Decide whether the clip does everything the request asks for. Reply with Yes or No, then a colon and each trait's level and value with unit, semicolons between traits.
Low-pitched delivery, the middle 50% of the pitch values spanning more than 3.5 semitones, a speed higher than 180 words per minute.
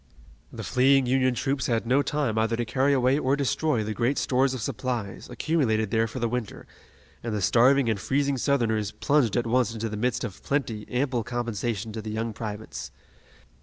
No: low, 120 Hz; average, 3.2 semitones; average, 190 wpm